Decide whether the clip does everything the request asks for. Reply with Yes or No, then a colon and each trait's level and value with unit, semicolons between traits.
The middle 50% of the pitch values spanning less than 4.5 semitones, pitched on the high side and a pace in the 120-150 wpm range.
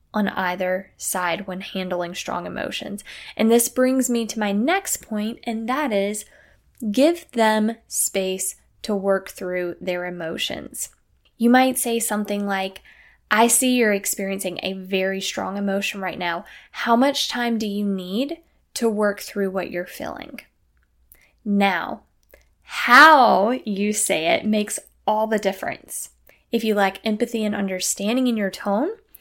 Yes: average, 3.5 semitones; high, 210 Hz; average, 145 wpm